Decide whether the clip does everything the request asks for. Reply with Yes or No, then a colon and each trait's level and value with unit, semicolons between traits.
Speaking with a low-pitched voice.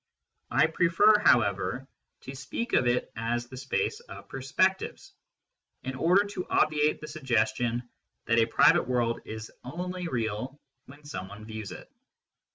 Yes: low, 130 Hz